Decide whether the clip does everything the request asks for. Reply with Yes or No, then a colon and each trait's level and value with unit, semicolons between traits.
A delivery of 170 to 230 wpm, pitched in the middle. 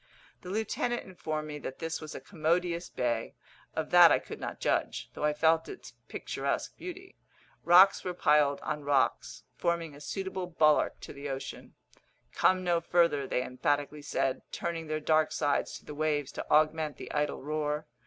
Yes: average, 175 wpm; medium, 155 Hz